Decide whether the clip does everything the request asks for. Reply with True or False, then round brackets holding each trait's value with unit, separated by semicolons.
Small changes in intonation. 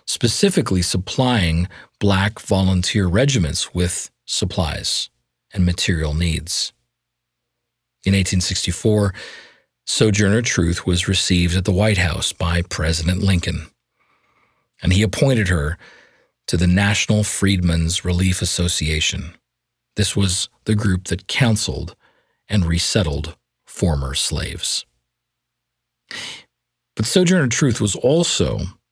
False (3.4 semitones)